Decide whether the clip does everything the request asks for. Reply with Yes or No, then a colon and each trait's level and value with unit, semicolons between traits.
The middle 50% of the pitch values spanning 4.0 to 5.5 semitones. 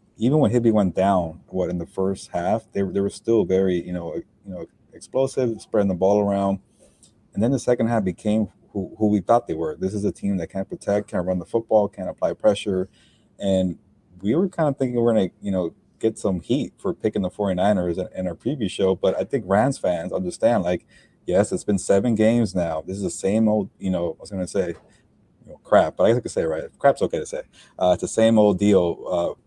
No: average, 3.1 semitones